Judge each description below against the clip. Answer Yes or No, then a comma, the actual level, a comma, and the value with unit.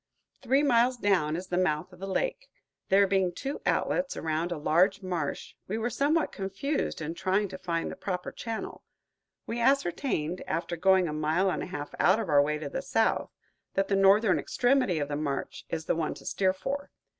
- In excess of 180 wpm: Yes, average, 200 wpm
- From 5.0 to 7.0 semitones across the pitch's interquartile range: Yes, wide, 5.5 semitones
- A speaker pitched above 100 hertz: Yes, high, 190 Hz